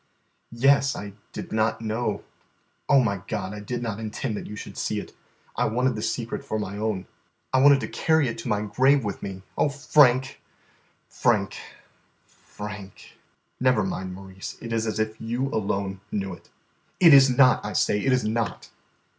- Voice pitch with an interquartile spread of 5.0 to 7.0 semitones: No, average, 3.9 semitones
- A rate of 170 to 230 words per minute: Yes, average, 180 wpm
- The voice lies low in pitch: Yes, low, 110 Hz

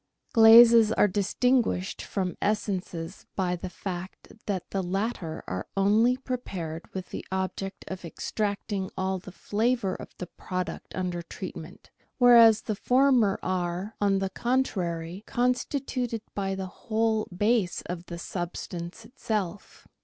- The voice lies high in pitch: Yes, high, 195 Hz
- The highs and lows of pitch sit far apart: No, average, 3.8 semitones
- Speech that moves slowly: Yes, slow, 130 wpm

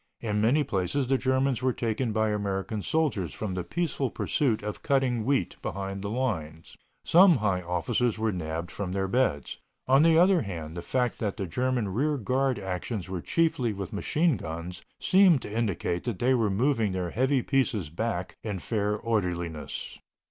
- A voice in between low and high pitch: No, low, 110 Hz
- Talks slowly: No, average, 175 wpm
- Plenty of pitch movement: Yes, wide, 5.8 semitones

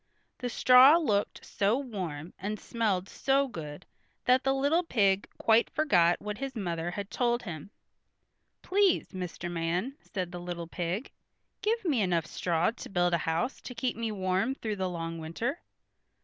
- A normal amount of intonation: No, wide, 6.4 semitones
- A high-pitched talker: Yes, high, 200 Hz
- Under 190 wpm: Yes, average, 165 wpm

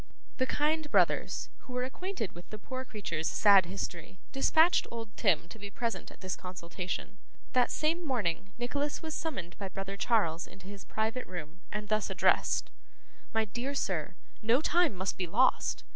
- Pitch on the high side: Yes, high, 215 Hz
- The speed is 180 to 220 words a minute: No, average, 170 wpm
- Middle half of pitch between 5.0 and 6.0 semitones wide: Yes, wide, 5.6 semitones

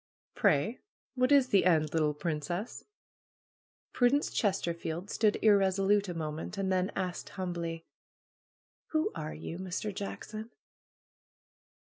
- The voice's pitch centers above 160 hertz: Yes, medium, 185 Hz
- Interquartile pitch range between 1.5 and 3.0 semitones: No, average, 4.0 semitones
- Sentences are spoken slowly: Yes, slow, 115 wpm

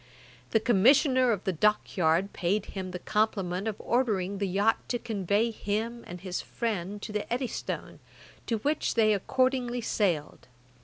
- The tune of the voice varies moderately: Yes, average, 3.7 semitones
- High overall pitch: Yes, high, 210 Hz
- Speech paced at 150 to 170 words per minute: Yes, average, 155 wpm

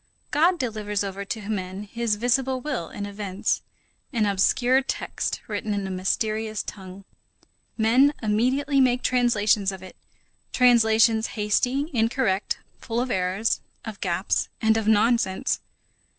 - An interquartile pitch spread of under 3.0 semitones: No, average, 3.4 semitones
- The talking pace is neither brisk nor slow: No, slow, 130 wpm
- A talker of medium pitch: No, high, 220 Hz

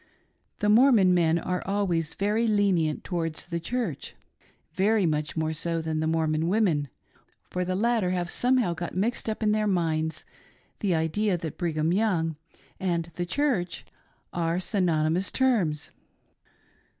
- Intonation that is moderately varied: Yes, average, 4.3 semitones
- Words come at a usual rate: Yes, average, 150 wpm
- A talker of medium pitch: Yes, medium, 175 Hz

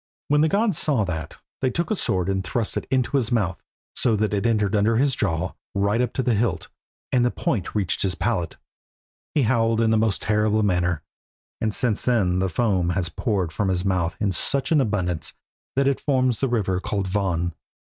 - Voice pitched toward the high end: No, low, 105 Hz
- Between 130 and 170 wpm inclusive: No, average, 200 wpm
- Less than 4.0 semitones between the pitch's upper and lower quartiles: No, average, 4.7 semitones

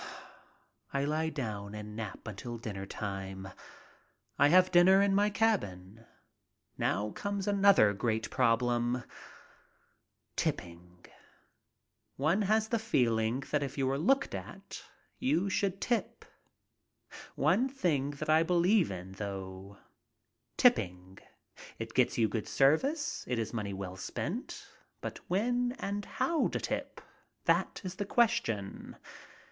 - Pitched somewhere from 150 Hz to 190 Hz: No, low, 135 Hz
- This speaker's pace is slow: Yes, slow, 130 wpm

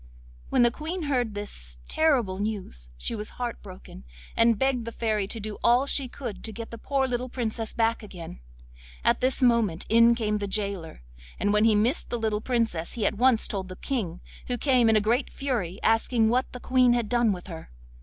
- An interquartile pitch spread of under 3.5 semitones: Yes, average, 3.1 semitones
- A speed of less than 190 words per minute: No, fast, 205 wpm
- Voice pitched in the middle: No, high, 225 Hz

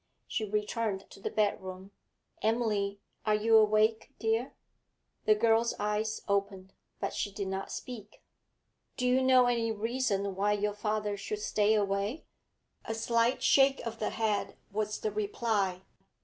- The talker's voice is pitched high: Yes, high, 215 Hz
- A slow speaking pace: No, average, 145 wpm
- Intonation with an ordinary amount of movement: No, narrow, 2.0 semitones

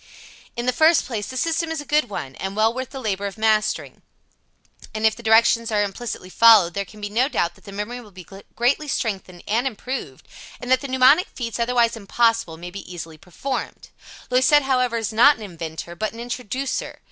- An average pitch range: Yes, average, 4.2 semitones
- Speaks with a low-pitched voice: No, high, 230 Hz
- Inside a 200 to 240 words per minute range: Yes, fast, 205 wpm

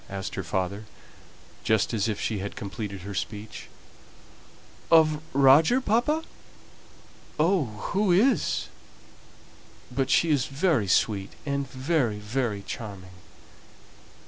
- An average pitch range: No, wide, 7.6 semitones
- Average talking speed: No, slow, 110 wpm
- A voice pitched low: Yes, low, 125 Hz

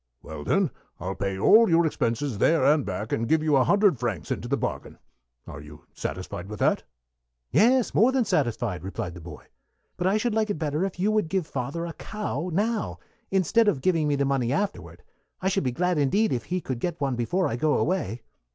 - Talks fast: Yes, fast, 215 wpm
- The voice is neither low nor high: Yes, medium, 155 Hz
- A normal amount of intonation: No, wide, 8.5 semitones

